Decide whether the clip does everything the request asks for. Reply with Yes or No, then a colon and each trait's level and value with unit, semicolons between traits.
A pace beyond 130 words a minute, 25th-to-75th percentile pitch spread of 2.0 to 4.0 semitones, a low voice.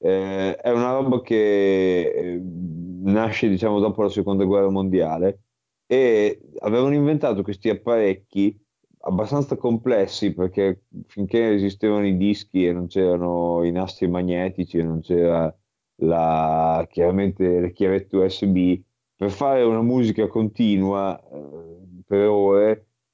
No: average, 120 wpm; average, 3.2 semitones; low, 100 Hz